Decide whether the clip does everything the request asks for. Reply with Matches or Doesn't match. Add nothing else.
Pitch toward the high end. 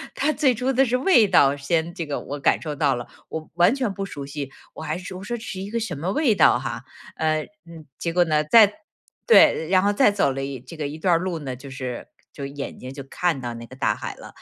Doesn't match